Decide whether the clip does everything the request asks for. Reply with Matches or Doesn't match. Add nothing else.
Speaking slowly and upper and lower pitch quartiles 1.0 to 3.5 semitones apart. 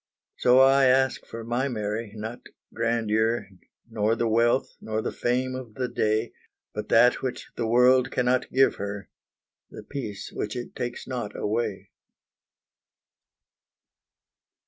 Matches